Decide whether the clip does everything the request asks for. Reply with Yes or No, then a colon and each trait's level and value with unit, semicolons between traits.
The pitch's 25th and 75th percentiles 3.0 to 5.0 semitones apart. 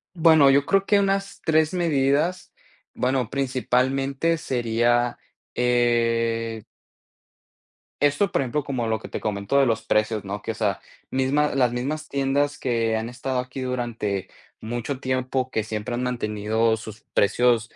Yes: average, 3.5 semitones